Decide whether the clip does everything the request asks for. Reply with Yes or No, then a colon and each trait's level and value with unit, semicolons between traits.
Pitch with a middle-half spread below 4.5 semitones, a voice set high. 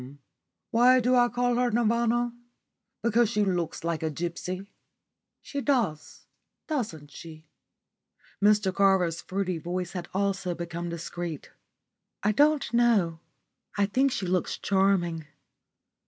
No: wide, 5.6 semitones; high, 195 Hz